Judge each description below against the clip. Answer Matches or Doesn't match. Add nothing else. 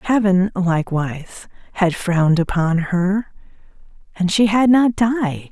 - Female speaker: Matches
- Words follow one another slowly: Matches